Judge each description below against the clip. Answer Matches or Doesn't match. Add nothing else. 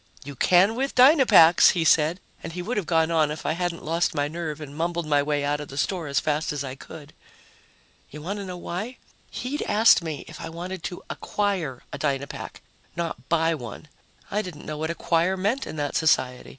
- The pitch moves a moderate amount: Matches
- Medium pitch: Matches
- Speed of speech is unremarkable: Doesn't match